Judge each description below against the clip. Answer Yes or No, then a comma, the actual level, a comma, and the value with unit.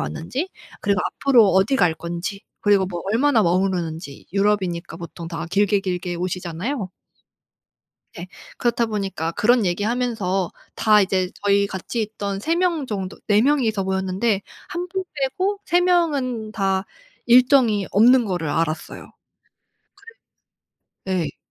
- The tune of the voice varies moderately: Yes, average, 4.9 semitones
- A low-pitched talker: No, high, 200 Hz